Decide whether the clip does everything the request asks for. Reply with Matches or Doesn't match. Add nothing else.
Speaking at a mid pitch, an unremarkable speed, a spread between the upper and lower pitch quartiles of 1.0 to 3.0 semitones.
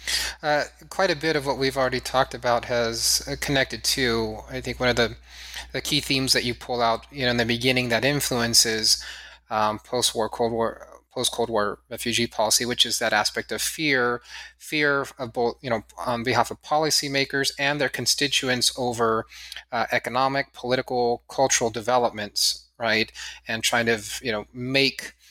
Doesn't match